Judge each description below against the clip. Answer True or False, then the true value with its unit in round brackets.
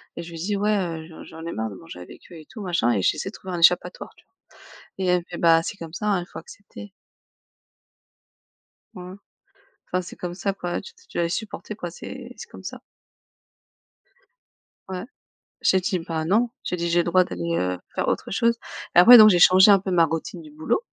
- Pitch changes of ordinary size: True (3.2 semitones)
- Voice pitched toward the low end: False (180 Hz)